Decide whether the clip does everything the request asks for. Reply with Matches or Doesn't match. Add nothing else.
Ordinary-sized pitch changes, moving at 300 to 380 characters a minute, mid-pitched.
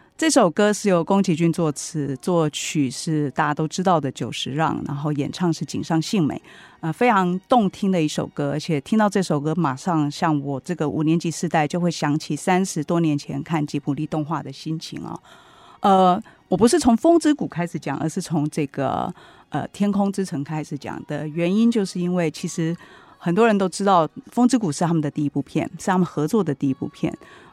Matches